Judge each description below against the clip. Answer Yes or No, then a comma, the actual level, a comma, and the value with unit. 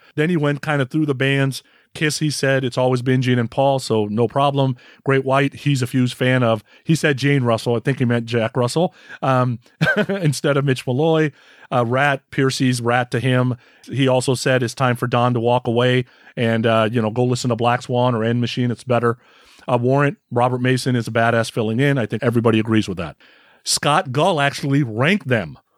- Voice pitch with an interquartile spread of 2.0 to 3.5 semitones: Yes, narrow, 2.6 semitones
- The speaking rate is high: Yes, fast, 215 wpm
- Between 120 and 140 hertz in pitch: Yes, low, 125 Hz